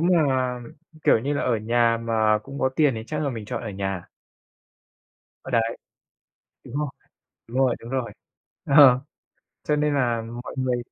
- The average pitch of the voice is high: No, low, 125 Hz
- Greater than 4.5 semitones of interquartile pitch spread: No, average, 3.4 semitones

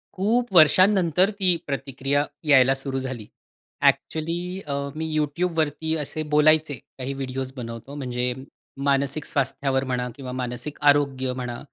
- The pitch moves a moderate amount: Yes, average, 3.1 semitones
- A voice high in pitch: No, medium, 140 Hz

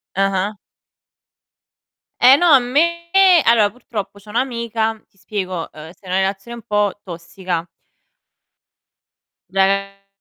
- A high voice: Yes, high, 200 Hz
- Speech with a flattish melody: No, average, 3.5 semitones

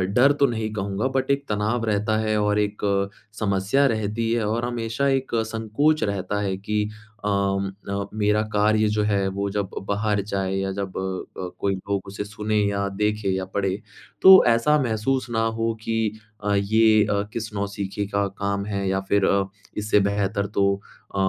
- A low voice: Yes, low, 105 Hz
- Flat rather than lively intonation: Yes, narrow, 2.1 semitones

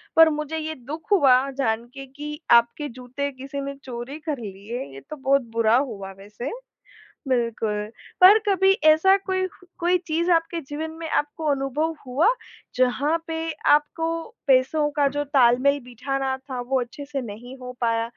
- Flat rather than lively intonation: No, average, 4.3 semitones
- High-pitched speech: Yes, very high, 275 Hz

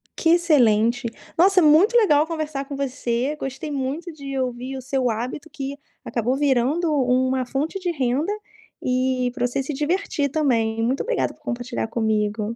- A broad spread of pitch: No, average, 3.7 semitones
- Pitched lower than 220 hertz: No, very high, 270 Hz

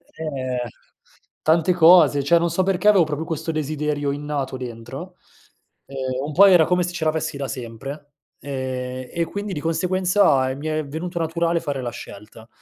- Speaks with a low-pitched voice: No, medium, 155 Hz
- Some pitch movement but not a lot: Yes, average, 4.1 semitones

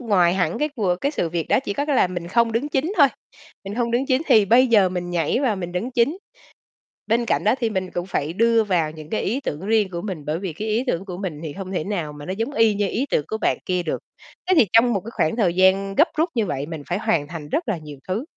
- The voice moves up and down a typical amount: Yes, average, 5.0 semitones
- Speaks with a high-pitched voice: Yes, high, 195 Hz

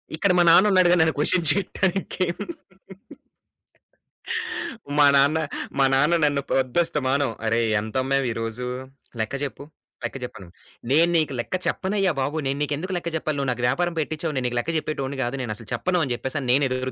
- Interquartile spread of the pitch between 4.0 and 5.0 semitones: Yes, average, 4.5 semitones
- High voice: No, medium, 140 Hz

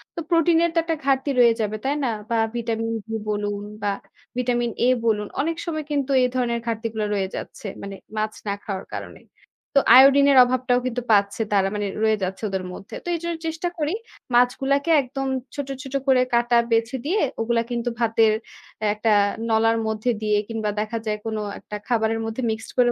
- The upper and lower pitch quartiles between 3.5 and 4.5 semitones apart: Yes, average, 3.8 semitones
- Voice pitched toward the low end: No, high, 230 Hz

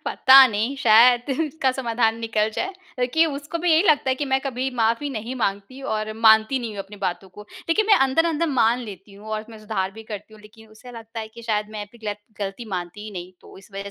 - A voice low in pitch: No, high, 225 Hz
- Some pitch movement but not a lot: Yes, average, 4.0 semitones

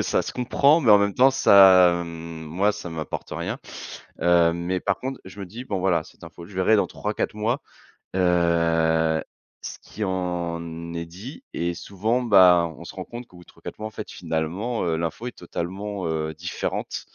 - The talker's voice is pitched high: No, very low, 90 Hz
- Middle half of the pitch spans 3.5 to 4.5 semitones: Yes, average, 3.8 semitones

